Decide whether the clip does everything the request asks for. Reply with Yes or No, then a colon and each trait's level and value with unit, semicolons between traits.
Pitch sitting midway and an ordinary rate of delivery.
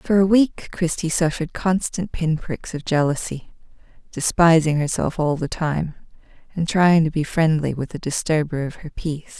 Yes: medium, 160 Hz; average, 165 wpm